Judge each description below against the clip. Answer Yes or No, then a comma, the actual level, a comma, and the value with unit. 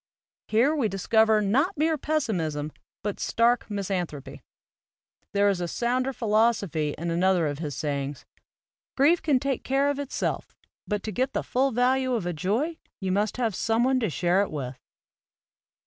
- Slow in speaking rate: No, average, 165 wpm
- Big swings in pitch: Yes, wide, 6.6 semitones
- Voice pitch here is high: Yes, high, 215 Hz